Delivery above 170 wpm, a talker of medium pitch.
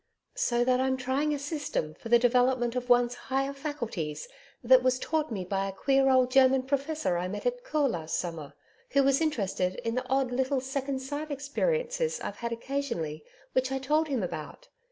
No: average, 190 wpm; very high, 260 Hz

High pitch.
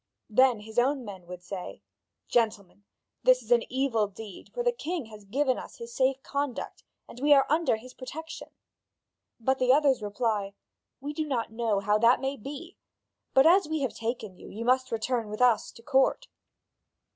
Yes: very high, 255 Hz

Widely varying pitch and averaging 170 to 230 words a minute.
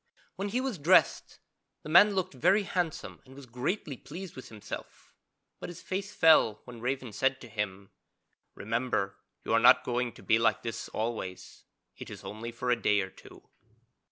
Yes: wide, 7.5 semitones; average, 180 wpm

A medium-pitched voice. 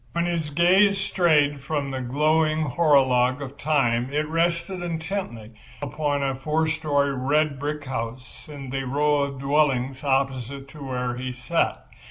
Yes: medium, 145 Hz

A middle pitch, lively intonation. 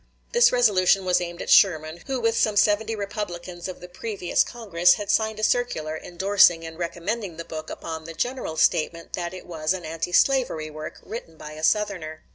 No: medium, 180 Hz; average, 4.5 semitones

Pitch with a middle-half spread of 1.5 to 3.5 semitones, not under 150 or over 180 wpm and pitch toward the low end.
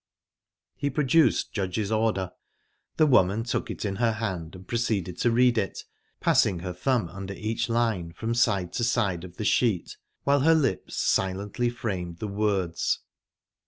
No: average, 4.3 semitones; average, 160 wpm; low, 110 Hz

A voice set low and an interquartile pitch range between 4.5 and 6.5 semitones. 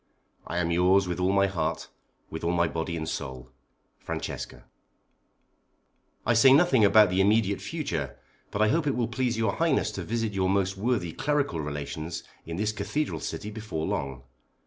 Yes: low, 100 Hz; average, 5.1 semitones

